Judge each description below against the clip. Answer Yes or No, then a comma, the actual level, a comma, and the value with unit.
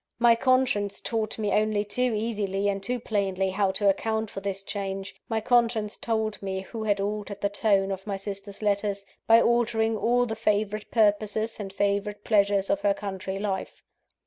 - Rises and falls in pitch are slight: Yes, narrow, 2.0 semitones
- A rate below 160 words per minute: No, average, 175 wpm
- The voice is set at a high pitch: Yes, high, 205 Hz